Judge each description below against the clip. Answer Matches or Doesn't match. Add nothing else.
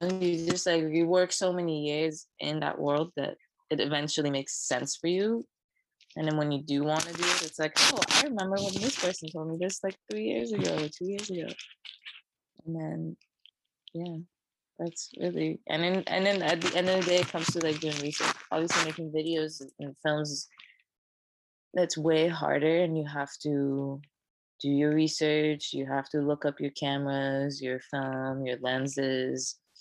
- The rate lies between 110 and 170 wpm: Doesn't match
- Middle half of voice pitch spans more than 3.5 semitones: Doesn't match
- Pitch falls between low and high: Matches